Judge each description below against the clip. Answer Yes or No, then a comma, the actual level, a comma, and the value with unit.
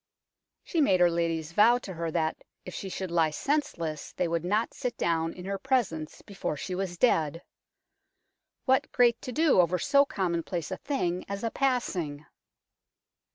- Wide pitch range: Yes, wide, 6.1 semitones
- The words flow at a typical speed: Yes, average, 165 wpm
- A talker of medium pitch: Yes, medium, 180 Hz